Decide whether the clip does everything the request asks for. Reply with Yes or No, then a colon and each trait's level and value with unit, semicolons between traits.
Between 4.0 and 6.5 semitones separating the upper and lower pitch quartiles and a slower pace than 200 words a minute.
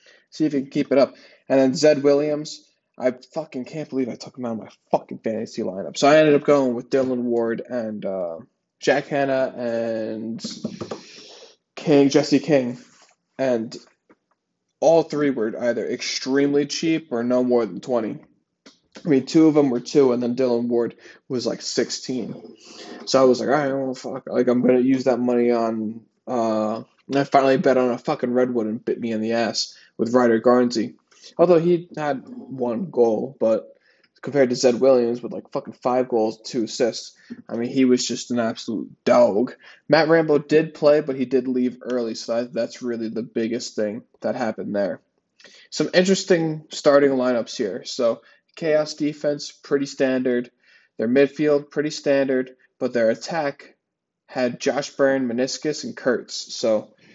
No: average, 3.5 semitones; average, 175 wpm